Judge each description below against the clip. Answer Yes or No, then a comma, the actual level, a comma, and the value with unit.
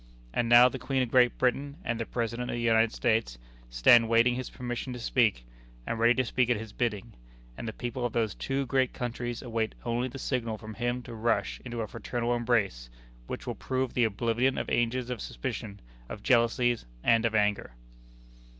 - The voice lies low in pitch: Yes, low, 120 Hz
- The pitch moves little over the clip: Yes, narrow, 1.7 semitones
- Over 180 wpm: Yes, average, 195 wpm